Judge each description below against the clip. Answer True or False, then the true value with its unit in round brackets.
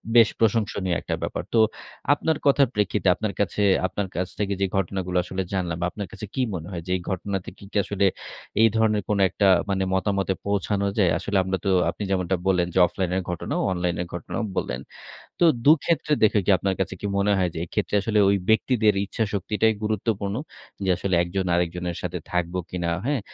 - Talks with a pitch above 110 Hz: False (100 Hz)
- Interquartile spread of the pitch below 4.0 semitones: True (2.7 semitones)